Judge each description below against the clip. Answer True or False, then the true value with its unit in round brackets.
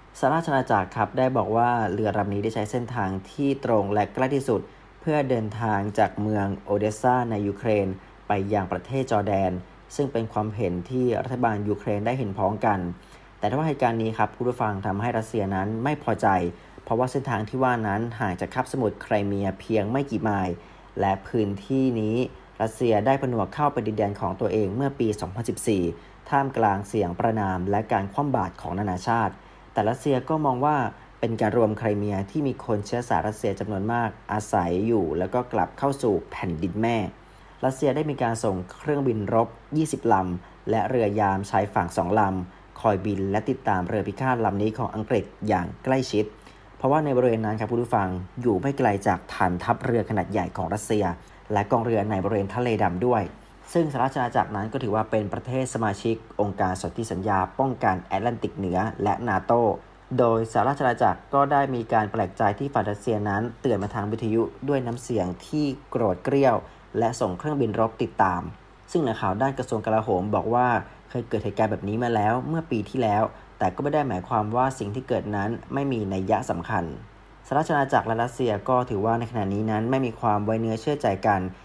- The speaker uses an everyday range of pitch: True (3.7 semitones)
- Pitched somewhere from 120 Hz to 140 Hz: False (110 Hz)